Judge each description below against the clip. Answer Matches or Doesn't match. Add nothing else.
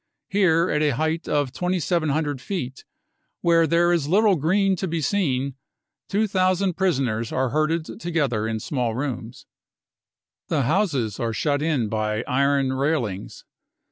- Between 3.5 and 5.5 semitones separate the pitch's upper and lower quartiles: Matches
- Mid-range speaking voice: Matches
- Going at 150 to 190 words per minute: Doesn't match